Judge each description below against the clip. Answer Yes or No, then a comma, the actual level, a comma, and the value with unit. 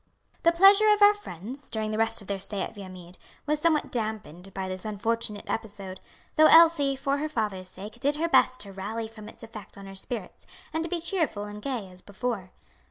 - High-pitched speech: Yes, high, 220 Hz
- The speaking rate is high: Yes, fast, 210 wpm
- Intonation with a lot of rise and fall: Yes, wide, 6.9 semitones